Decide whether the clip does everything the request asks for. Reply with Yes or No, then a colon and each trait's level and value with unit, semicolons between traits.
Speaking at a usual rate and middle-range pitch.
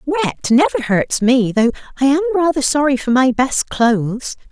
No: average, 175 wpm; very high, 265 Hz